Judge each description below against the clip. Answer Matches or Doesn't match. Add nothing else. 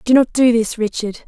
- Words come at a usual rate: Doesn't match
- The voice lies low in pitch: Doesn't match